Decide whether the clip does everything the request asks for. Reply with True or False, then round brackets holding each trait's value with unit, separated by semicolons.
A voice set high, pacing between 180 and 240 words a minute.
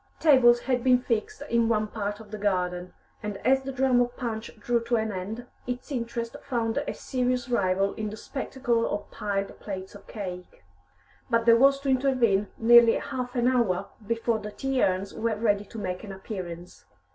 True (230 Hz; 185 wpm)